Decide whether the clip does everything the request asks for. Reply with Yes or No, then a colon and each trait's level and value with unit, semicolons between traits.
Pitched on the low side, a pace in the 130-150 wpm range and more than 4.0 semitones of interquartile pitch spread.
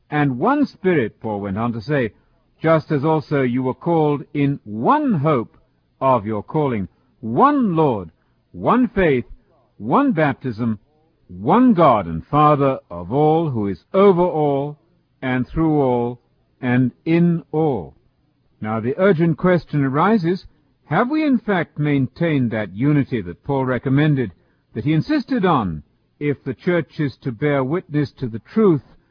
No: medium, 145 Hz; average, 145 wpm; average, 5.2 semitones